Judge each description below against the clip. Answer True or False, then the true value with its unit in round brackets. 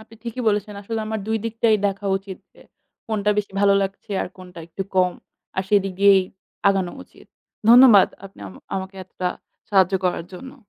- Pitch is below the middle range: False (200 Hz)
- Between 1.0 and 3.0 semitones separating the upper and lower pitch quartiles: True (2.4 semitones)